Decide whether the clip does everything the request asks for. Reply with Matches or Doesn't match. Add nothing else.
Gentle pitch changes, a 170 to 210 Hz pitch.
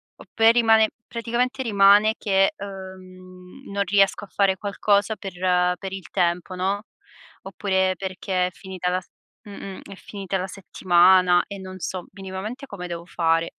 Matches